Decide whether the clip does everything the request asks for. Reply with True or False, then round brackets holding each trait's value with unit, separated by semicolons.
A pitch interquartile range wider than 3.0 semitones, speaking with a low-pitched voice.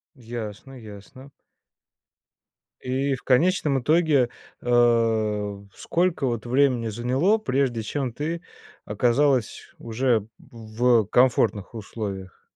True (3.7 semitones; 120 Hz)